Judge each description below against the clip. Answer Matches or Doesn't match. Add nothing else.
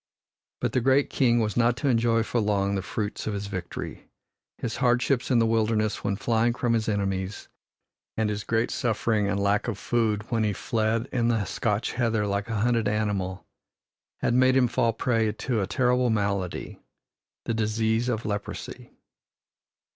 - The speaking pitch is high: Doesn't match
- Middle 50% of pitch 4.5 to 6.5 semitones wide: Doesn't match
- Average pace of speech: Matches